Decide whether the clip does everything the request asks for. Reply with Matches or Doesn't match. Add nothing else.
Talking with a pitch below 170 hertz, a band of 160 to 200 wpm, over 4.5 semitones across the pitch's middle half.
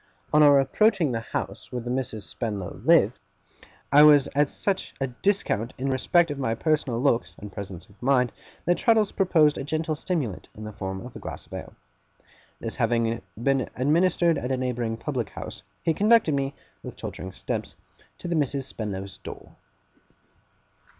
Matches